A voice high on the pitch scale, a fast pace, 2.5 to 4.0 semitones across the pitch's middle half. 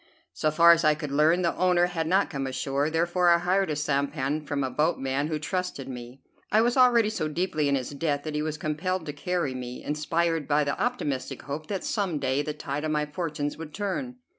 No: medium, 155 Hz; fast, 220 wpm; average, 3.6 semitones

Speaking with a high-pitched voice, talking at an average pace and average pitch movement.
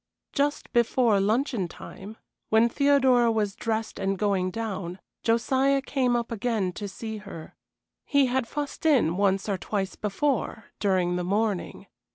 Yes: high, 220 Hz; average, 145 wpm; average, 4.2 semitones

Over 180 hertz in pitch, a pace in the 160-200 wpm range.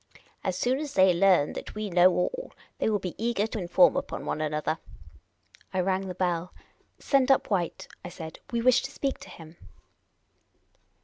Yes: high, 190 Hz; average, 190 wpm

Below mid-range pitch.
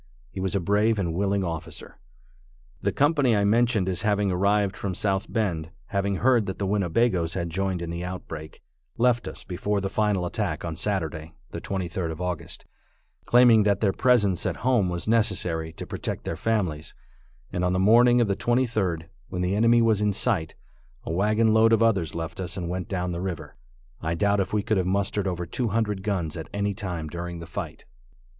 Yes: very low, 95 Hz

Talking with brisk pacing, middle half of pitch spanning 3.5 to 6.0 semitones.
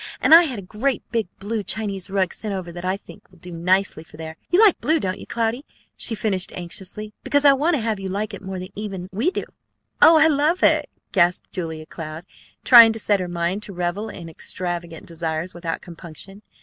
Yes: fast, 215 wpm; average, 4.4 semitones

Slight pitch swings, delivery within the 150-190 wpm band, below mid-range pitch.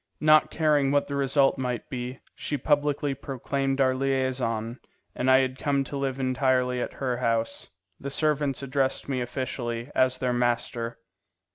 Yes: narrow, 1.8 semitones; average, 155 wpm; low, 130 Hz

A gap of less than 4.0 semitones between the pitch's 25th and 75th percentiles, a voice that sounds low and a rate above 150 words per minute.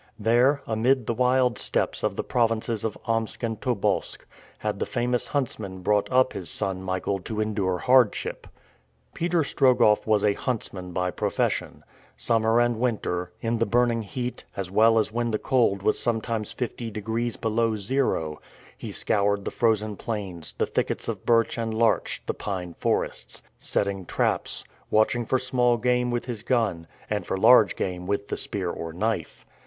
Yes: average, 3.3 semitones; low, 110 Hz; average, 165 wpm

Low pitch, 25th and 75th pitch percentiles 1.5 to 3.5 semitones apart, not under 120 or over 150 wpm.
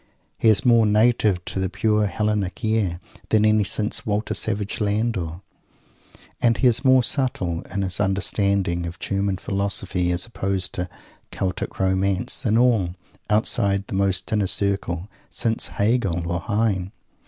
Yes: low, 100 Hz; narrow, 2.6 semitones; average, 145 wpm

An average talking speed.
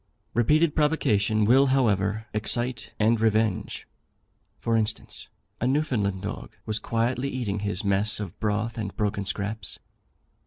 No: slow, 125 wpm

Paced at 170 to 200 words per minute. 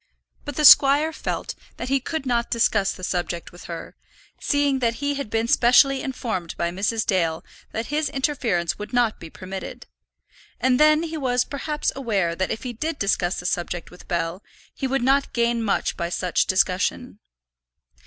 Yes: average, 175 wpm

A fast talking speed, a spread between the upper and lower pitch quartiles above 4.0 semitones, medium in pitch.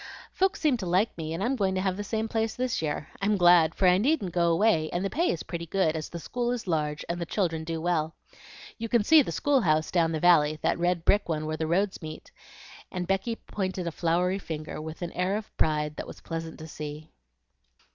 Yes: fast, 240 wpm; average, 4.4 semitones; medium, 175 Hz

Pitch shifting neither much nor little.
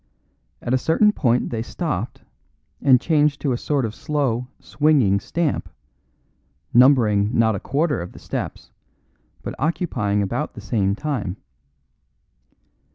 No: wide, 5.9 semitones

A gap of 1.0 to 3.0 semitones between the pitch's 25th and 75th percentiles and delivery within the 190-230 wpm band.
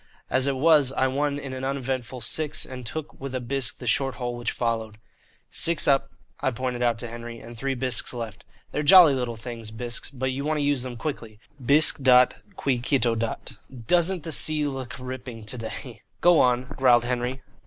Yes: average, 2.7 semitones; average, 195 wpm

